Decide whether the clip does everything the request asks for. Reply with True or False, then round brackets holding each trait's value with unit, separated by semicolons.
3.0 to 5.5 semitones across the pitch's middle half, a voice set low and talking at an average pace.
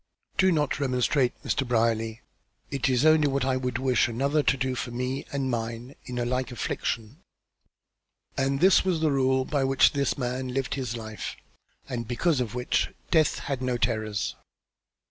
False (2.4 semitones; 130 Hz; 170 wpm)